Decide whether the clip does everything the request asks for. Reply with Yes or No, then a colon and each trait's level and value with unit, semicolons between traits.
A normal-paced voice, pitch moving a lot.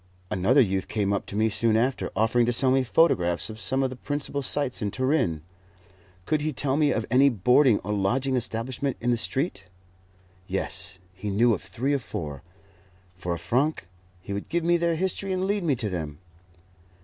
Yes: average, 195 wpm; wide, 5.9 semitones